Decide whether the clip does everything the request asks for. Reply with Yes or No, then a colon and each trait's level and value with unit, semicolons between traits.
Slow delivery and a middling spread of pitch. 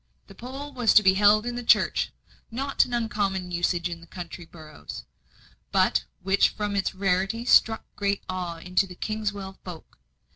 No: average, 160 wpm; average, 3.6 semitones